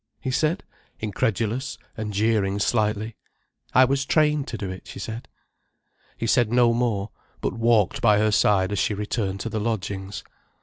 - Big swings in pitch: No, average, 2.9 semitones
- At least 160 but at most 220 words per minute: Yes, average, 165 wpm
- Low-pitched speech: Yes, low, 110 Hz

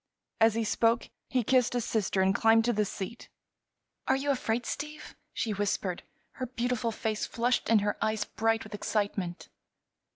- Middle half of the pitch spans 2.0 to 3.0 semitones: Yes, narrow, 2.6 semitones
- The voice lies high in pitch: Yes, high, 225 Hz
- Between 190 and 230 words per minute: No, average, 165 wpm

